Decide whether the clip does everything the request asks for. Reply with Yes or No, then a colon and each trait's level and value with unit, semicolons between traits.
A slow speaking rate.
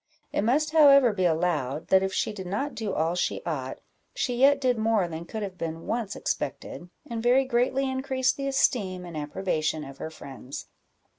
No: average, 190 wpm